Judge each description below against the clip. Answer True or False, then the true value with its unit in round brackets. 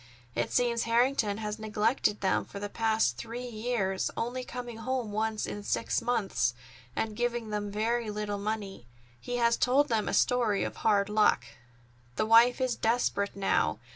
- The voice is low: False (220 Hz)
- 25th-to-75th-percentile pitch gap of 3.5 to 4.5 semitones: False (2.7 semitones)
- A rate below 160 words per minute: False (165 wpm)